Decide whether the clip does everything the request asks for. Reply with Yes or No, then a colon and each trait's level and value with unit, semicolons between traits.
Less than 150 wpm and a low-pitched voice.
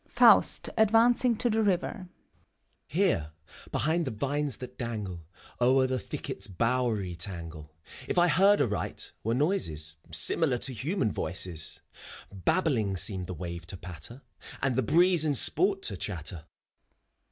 Yes: average, 140 wpm; low, 125 Hz